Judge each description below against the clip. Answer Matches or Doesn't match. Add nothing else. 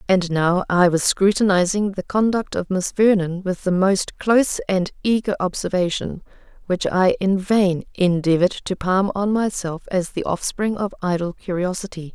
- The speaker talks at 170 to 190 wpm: Doesn't match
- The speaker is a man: Doesn't match